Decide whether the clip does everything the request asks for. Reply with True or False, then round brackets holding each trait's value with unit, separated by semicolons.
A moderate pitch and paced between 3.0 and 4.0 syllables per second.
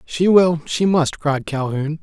True (160 Hz; 3.7 syllables/s)